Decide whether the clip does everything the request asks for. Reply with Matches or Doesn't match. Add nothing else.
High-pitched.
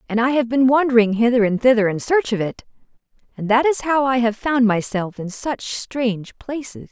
Matches